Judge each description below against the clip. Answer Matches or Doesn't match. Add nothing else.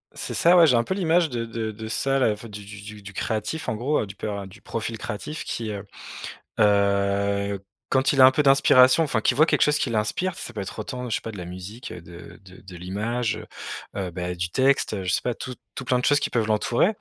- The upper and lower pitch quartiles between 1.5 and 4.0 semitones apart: Doesn't match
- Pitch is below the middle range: Matches